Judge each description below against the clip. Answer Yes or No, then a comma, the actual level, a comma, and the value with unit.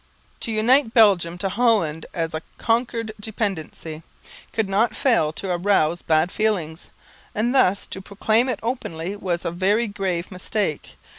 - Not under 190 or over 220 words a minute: No, average, 150 wpm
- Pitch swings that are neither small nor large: Yes, average, 4.7 semitones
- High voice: Yes, high, 200 Hz